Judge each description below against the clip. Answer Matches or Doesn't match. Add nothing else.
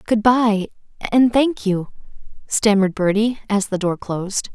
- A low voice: Doesn't match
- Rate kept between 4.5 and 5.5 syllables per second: Matches